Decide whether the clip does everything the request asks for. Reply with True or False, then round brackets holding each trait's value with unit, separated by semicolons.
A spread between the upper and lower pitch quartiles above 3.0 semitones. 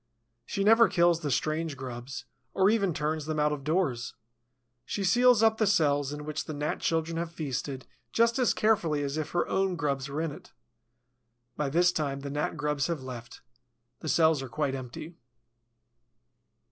True (3.8 semitones)